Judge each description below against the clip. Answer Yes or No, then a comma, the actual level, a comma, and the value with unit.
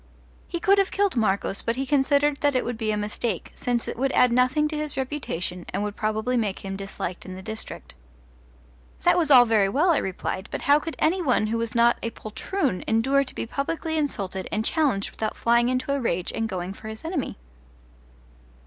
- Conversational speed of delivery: No, fast, 210 wpm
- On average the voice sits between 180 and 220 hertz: No, high, 240 Hz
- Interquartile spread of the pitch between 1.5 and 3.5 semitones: No, average, 5.1 semitones